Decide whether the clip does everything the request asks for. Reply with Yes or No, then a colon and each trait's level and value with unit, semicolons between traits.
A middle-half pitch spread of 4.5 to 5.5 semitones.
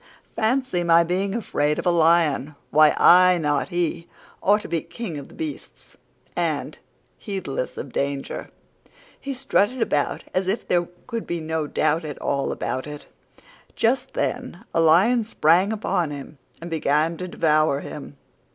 Yes: average, 5.0 semitones